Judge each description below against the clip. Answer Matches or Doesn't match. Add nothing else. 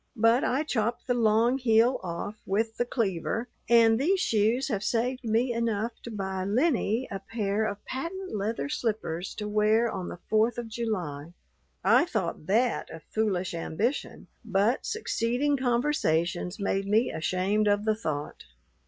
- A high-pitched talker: Matches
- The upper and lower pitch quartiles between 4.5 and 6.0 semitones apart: Doesn't match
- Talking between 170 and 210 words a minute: Doesn't match